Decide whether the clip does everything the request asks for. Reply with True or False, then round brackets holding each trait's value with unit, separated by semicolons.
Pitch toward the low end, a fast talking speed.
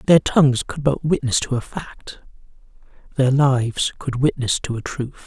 False (130 Hz; 170 wpm)